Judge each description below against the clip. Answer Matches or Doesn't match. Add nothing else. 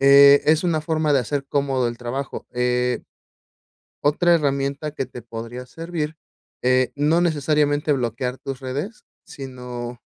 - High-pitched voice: Doesn't match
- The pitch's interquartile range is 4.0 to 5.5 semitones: Doesn't match